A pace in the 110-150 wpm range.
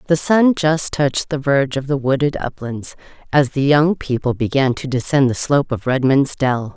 No: average, 195 wpm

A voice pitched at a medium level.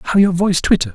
Yes: medium, 180 Hz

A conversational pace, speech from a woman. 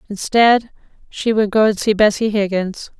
Yes: average, 160 wpm; female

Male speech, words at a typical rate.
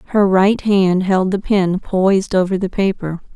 No: female; average, 180 wpm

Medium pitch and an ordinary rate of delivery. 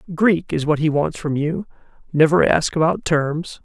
Yes: medium, 160 Hz; average, 165 wpm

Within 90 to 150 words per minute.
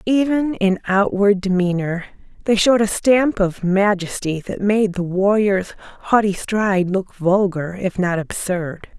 Yes: average, 140 wpm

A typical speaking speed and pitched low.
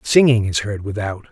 Yes: average, 180 wpm; low, 110 Hz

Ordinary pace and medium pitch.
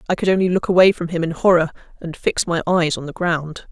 No: fast, 260 wpm; medium, 170 Hz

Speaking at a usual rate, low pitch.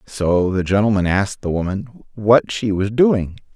Yes: average, 170 wpm; low, 105 Hz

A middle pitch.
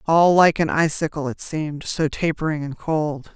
Yes: medium, 155 Hz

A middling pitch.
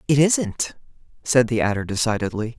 No: low, 120 Hz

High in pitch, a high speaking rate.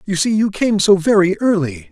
Yes: high, 195 Hz; fast, 220 wpm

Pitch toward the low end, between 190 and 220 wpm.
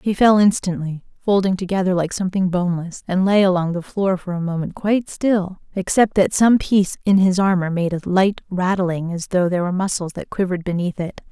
No: medium, 185 Hz; average, 200 wpm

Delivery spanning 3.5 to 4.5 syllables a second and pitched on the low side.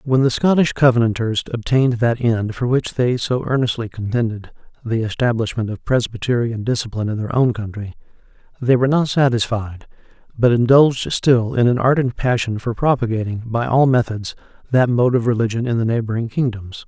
No: 5.5 syllables/s; low, 120 Hz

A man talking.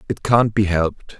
Yes: male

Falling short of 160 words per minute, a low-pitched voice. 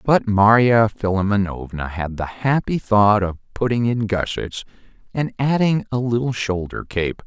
Yes: average, 140 wpm; low, 110 Hz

